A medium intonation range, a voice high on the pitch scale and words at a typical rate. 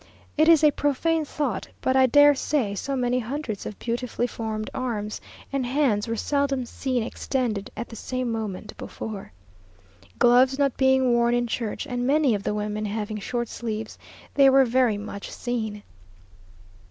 Yes: average, 3.6 semitones; high, 245 Hz; average, 165 wpm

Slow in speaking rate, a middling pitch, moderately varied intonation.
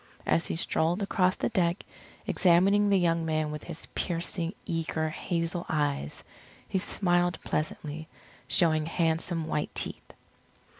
No: slow, 130 wpm; medium, 165 Hz; narrow, 2.1 semitones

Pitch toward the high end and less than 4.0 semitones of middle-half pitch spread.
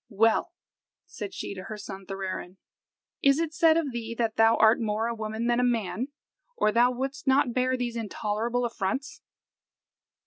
Yes: high, 230 Hz; average, 3.0 semitones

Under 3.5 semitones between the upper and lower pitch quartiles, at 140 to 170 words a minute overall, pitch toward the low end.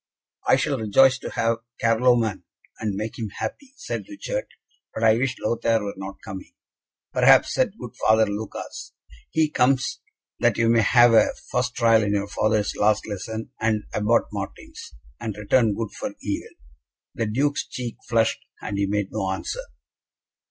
Yes: average, 2.7 semitones; average, 160 wpm; low, 110 Hz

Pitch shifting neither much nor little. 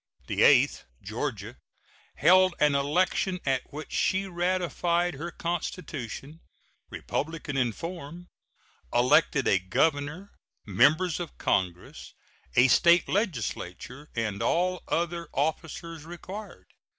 Yes: average, 4.3 semitones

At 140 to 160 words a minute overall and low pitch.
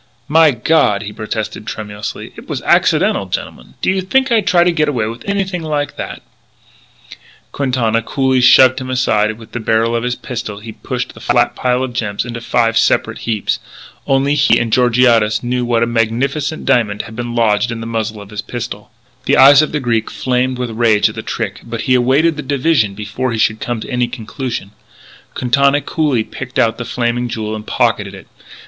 No: average, 200 wpm; low, 120 Hz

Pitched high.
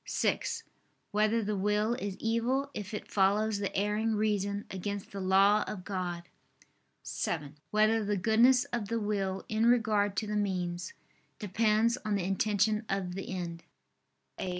Yes: high, 210 Hz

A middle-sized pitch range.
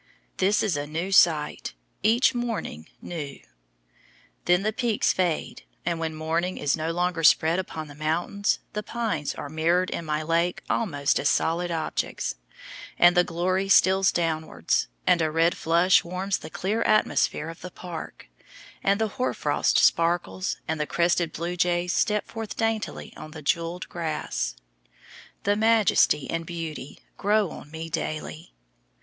Yes: average, 3.3 semitones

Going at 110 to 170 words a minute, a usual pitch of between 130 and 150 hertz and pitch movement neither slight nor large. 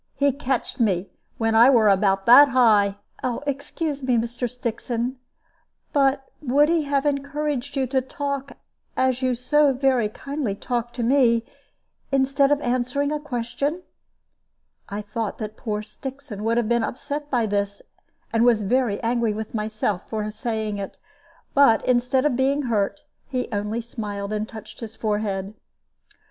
No: average, 150 wpm; high, 240 Hz; average, 4.1 semitones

